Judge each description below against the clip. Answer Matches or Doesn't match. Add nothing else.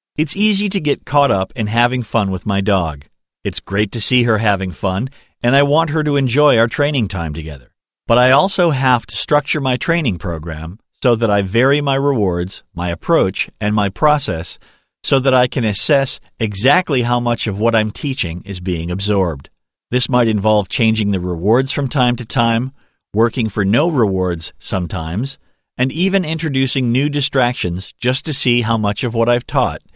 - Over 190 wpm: Doesn't match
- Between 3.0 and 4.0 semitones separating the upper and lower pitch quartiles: Doesn't match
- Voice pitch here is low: Matches